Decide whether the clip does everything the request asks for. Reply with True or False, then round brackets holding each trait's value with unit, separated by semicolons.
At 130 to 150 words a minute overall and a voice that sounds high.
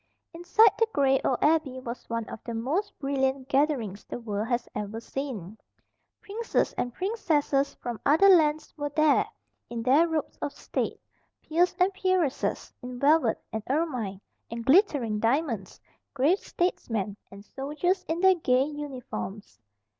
True (145 wpm; 275 Hz)